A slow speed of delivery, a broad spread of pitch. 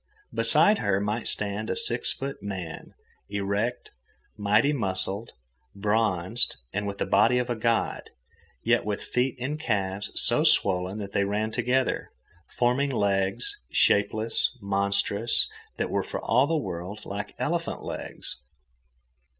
No: slow, 130 wpm; average, 3.4 semitones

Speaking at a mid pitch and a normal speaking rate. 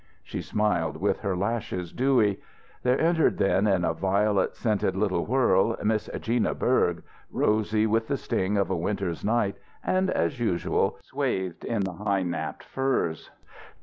No: low, 105 Hz; average, 150 wpm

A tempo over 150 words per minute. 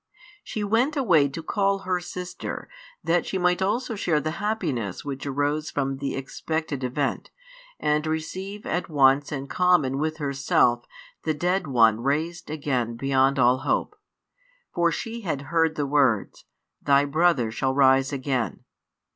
No: average, 145 wpm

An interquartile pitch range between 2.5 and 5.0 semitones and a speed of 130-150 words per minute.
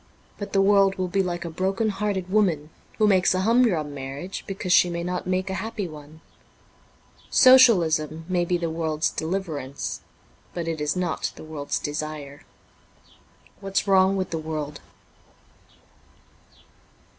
Yes: average, 3.8 semitones; average, 145 wpm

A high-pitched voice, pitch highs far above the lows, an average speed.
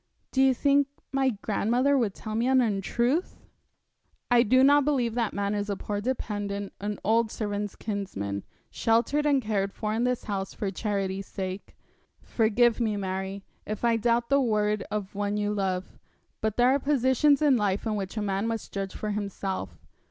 No: high, 215 Hz; average, 3.4 semitones; average, 180 wpm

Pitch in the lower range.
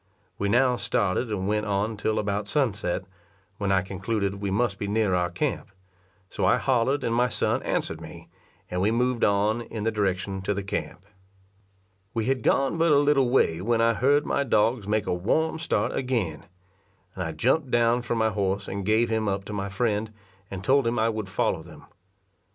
Yes: low, 110 Hz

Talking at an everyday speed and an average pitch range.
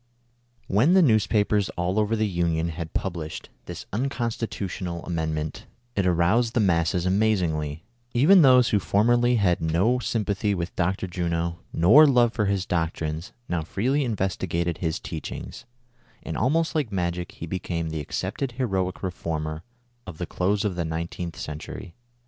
Yes: average, 150 wpm; average, 4.7 semitones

